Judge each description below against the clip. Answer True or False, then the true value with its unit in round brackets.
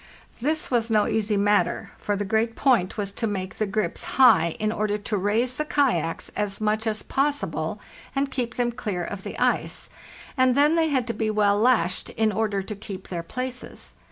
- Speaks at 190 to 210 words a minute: True (195 wpm)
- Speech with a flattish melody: False (3.5 semitones)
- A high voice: True (220 Hz)